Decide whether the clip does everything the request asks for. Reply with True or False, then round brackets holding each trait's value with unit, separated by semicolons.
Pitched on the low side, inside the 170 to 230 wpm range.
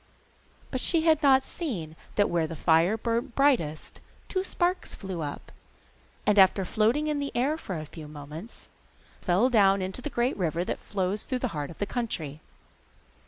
False (205 Hz; 175 wpm)